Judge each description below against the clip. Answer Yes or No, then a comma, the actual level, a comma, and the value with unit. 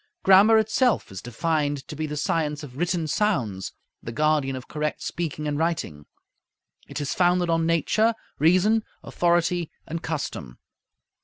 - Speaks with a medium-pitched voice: Yes, medium, 160 Hz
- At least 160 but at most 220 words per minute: No, average, 145 wpm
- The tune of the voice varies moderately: Yes, average, 3.3 semitones